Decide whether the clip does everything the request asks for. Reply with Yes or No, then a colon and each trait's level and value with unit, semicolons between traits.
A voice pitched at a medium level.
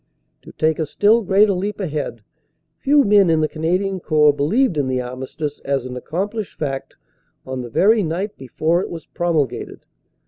Yes: medium, 160 Hz